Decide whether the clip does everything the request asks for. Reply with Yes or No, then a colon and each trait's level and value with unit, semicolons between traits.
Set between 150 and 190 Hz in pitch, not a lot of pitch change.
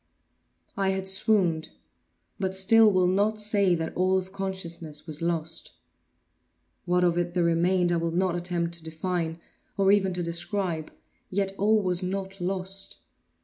Yes: medium, 185 Hz; narrow, 2.3 semitones